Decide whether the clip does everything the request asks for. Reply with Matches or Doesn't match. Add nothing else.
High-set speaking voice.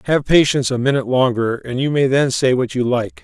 Doesn't match